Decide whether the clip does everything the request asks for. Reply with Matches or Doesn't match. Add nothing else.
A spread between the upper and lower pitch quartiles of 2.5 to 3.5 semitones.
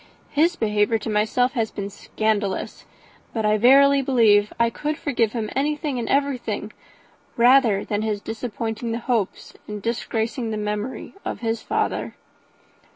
Matches